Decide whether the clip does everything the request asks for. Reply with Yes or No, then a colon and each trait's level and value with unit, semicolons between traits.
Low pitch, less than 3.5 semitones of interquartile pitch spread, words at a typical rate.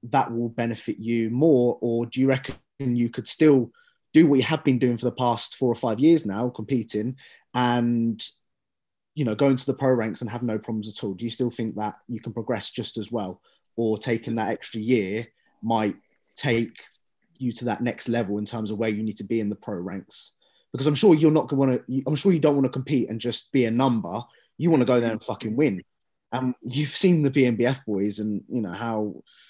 No: low, 120 Hz; average, 3.0 semitones; fast, 235 wpm